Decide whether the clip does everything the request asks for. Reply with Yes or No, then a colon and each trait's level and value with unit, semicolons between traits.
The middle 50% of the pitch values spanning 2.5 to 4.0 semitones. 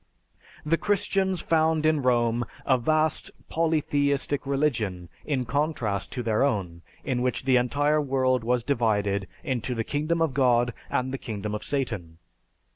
No: average, 4.4 semitones